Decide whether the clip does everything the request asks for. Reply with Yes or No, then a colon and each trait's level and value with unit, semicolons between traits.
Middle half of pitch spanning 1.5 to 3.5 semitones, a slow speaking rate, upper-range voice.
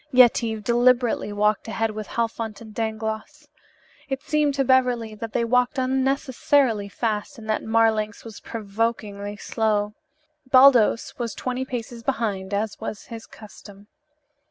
Yes: average, 2.8 semitones; slow, 130 wpm; high, 225 Hz